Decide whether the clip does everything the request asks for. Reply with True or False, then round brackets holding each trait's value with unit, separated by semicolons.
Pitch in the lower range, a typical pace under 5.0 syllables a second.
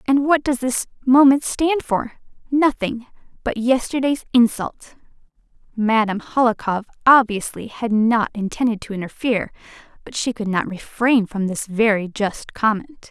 False (235 Hz; 4.6 syllables/s)